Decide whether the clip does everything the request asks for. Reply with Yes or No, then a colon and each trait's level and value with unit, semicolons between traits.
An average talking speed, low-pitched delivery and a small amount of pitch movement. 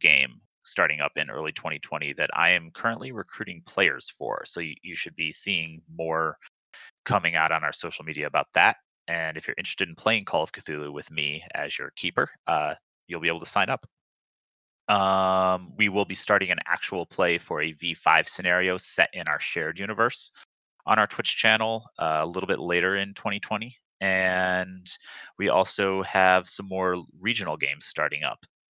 Yes: average, 180 wpm; very low, 95 Hz; narrow, 2.3 semitones